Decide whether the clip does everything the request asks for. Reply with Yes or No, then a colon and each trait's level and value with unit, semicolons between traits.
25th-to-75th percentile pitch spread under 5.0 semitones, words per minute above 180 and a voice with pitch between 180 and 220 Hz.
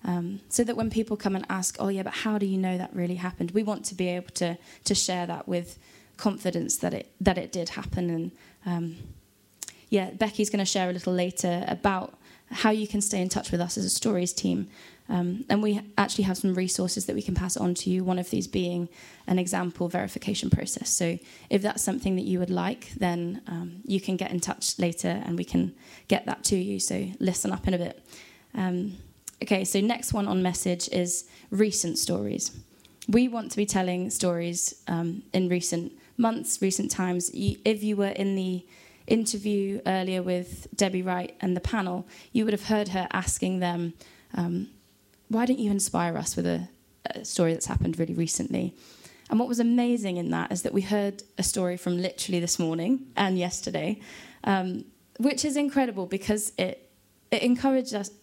Yes: average, 3.0 semitones; average, 200 wpm; high, 190 Hz